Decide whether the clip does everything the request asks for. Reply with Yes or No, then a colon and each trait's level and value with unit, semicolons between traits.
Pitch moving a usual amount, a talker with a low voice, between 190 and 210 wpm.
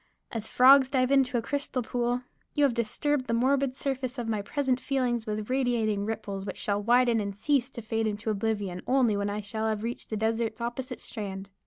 No: average, 3.3 semitones; high, 235 Hz; average, 200 wpm